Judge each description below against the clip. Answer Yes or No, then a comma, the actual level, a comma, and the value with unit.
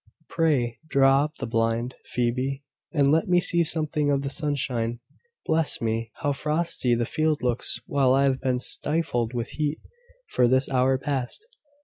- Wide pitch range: No, average, 3.7 semitones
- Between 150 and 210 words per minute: Yes, average, 160 wpm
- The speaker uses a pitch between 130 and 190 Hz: Yes, low, 135 Hz